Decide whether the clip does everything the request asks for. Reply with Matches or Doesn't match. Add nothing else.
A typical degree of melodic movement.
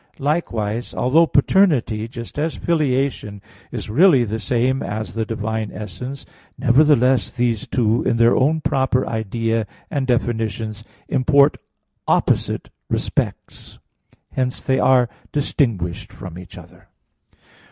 Matches